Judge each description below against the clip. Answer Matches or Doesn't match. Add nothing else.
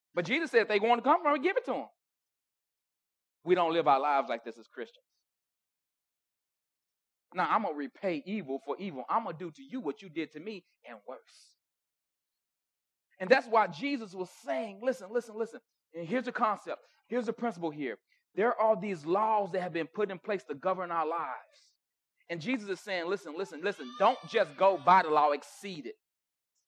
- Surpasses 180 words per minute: Matches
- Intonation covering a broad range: Matches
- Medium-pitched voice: Doesn't match